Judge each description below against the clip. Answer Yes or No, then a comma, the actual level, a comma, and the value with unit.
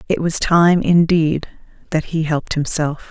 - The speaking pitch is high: No, medium, 160 Hz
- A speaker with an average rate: Yes, average, 155 wpm